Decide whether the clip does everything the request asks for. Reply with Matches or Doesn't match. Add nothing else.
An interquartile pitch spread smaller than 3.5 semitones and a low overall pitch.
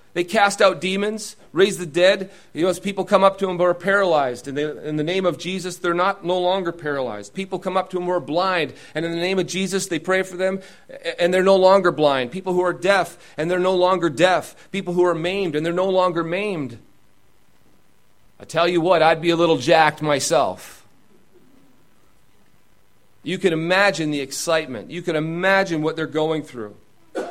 Doesn't match